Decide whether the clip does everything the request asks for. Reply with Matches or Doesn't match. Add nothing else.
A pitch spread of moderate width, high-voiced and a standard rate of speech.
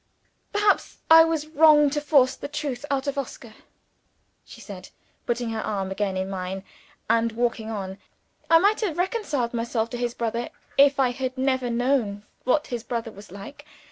Matches